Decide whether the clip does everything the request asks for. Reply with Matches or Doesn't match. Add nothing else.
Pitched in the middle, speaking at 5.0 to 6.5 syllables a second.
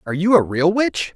Matches